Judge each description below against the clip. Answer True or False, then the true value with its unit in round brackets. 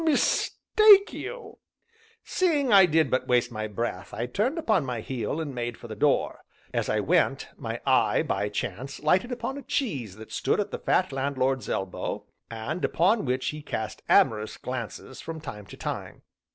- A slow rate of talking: False (175 wpm)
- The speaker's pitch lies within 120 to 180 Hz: True (135 Hz)